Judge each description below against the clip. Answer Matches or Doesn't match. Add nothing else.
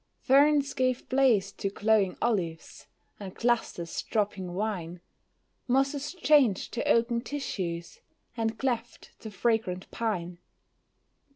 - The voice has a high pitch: Matches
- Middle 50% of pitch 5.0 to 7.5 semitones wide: Matches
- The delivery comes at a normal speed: Doesn't match